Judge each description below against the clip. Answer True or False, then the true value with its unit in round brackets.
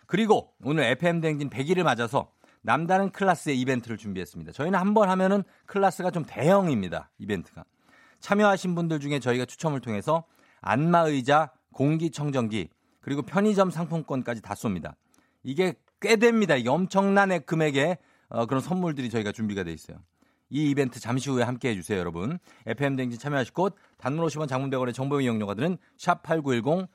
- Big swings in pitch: True (6.2 semitones)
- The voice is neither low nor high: True (145 Hz)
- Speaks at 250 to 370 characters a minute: False (380 characters per minute)